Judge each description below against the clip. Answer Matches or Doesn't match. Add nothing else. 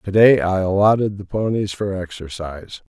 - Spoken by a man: Matches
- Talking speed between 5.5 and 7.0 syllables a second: Doesn't match